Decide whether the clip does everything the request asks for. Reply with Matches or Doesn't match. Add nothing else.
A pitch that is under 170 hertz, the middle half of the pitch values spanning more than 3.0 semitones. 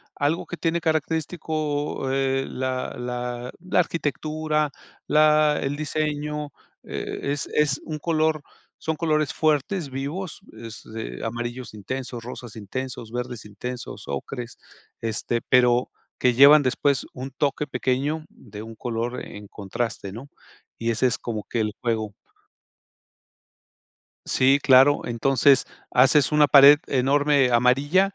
Matches